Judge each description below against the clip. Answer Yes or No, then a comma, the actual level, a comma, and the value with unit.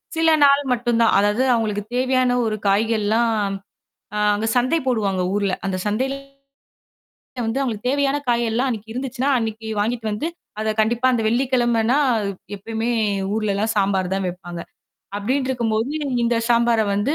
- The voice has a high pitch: Yes, high, 225 Hz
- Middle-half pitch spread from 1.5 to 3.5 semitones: Yes, average, 3.2 semitones